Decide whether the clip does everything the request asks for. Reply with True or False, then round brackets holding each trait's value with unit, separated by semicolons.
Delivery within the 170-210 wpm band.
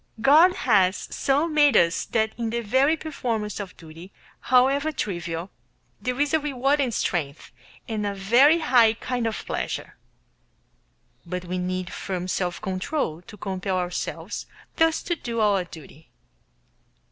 False (145 wpm)